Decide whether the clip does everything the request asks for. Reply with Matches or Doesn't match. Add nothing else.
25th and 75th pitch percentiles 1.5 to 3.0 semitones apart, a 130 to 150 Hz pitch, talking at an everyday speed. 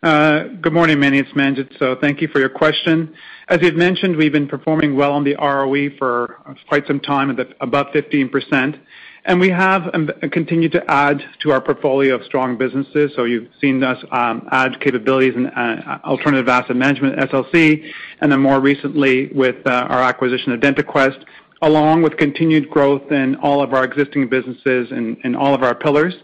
Matches